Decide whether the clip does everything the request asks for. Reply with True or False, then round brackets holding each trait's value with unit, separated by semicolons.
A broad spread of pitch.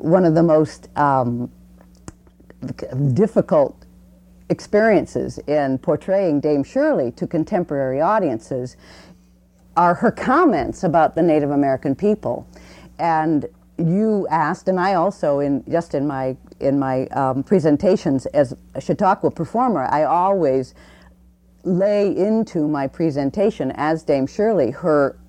True (6.1 semitones)